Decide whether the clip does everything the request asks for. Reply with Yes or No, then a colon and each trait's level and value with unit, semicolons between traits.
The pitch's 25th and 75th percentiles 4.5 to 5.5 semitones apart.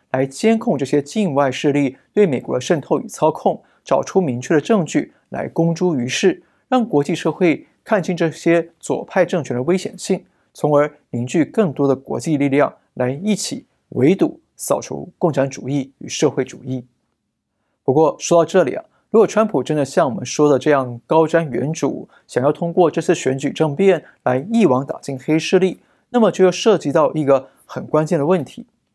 Yes: average, 5.1 semitones